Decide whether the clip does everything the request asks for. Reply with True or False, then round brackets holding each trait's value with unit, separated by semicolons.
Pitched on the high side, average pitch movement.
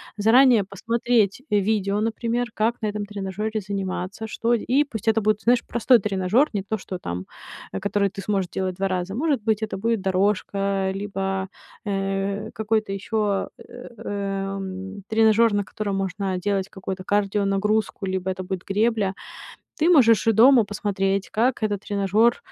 False (205 Hz; 2.3 semitones)